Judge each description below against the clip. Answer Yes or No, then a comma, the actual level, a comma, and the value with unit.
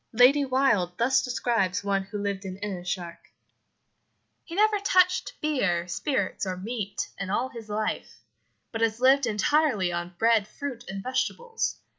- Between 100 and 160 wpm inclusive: Yes, average, 150 wpm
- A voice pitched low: No, high, 220 Hz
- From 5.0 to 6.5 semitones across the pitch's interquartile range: Yes, wide, 5.4 semitones